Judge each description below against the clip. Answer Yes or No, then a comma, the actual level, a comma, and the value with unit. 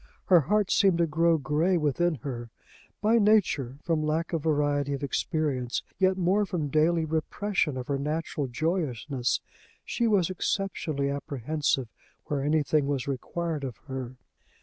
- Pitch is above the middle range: No, medium, 155 Hz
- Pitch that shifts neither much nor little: Yes, average, 3.7 semitones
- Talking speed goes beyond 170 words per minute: No, average, 145 wpm